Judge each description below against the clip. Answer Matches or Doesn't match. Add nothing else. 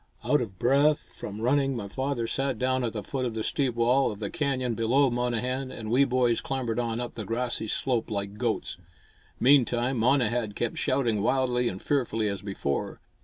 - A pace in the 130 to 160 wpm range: Doesn't match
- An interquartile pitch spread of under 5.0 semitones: Matches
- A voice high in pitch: Doesn't match